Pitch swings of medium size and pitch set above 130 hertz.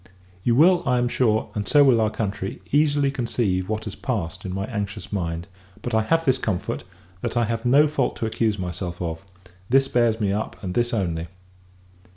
No: average, 4.4 semitones; low, 110 Hz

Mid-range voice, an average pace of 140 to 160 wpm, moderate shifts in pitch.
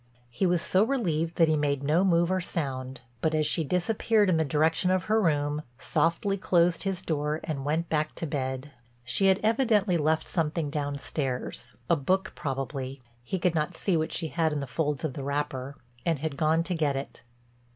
No: medium, 155 Hz; average, 190 wpm; average, 3.7 semitones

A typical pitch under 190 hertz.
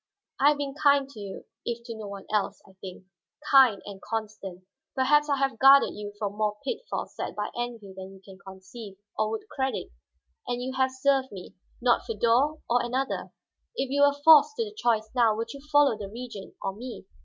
No: high, 235 Hz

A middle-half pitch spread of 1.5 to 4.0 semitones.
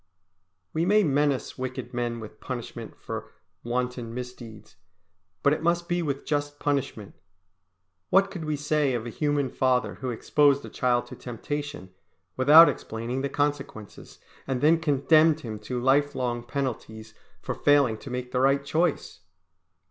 Yes: average, 3.3 semitones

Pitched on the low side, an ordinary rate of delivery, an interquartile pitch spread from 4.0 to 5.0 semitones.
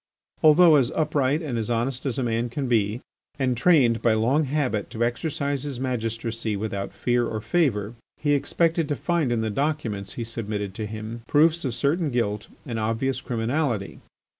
Yes: low, 120 Hz; average, 170 wpm; average, 4.5 semitones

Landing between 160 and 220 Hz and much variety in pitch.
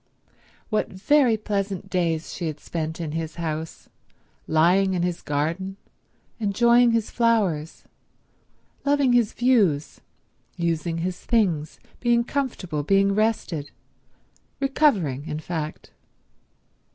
Yes: medium, 185 Hz; wide, 6.1 semitones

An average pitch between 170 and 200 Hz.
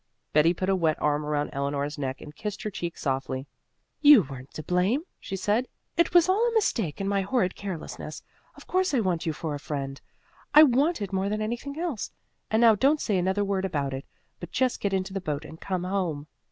Yes: high, 190 Hz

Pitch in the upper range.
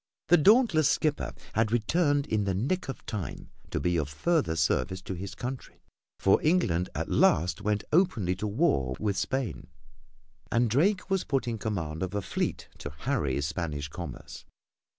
No: low, 105 Hz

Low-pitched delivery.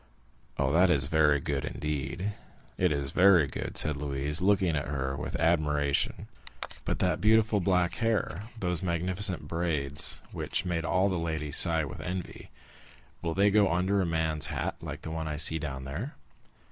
Yes: very low, 80 Hz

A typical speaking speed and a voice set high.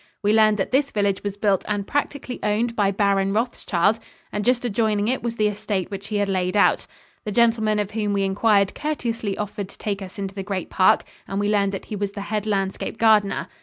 No: fast, 220 wpm; high, 205 Hz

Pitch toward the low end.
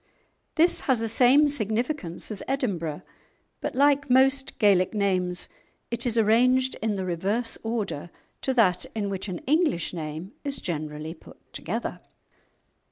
No: high, 220 Hz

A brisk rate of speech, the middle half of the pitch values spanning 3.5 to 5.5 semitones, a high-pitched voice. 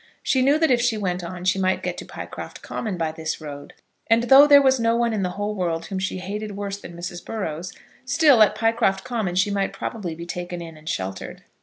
Yes: fast, 230 wpm; average, 4.7 semitones; high, 195 Hz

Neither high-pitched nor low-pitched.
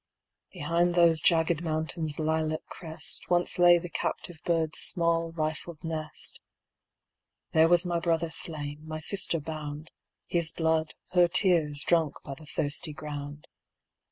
Yes: medium, 160 Hz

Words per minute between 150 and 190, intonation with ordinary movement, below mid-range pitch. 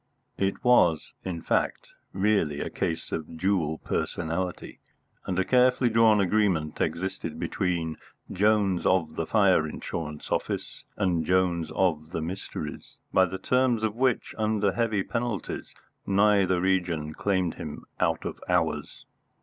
No: slow, 135 wpm; average, 4.1 semitones; very low, 95 Hz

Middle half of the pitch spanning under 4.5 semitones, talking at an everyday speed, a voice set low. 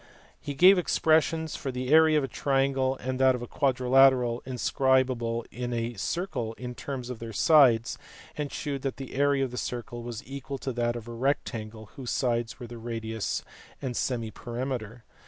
Yes: narrow, 2.5 semitones; average, 175 wpm; low, 125 Hz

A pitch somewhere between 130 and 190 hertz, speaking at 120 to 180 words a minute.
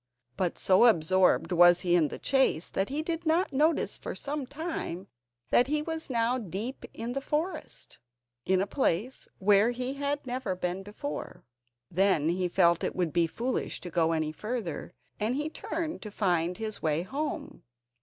No: high, 210 Hz; average, 175 wpm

